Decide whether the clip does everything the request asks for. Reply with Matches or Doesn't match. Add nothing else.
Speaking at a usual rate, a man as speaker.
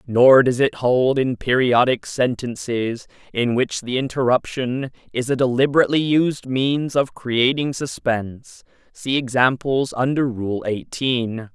Doesn't match